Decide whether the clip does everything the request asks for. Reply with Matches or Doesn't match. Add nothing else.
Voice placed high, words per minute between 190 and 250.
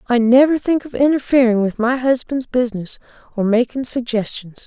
Doesn't match